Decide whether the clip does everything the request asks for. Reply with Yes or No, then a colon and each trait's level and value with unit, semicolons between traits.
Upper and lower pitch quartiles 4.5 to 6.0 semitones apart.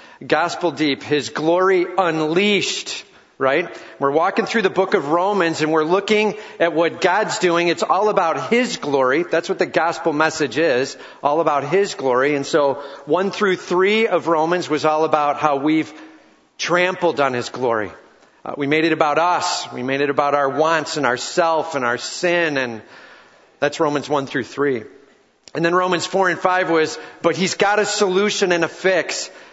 No: average, 3.5 semitones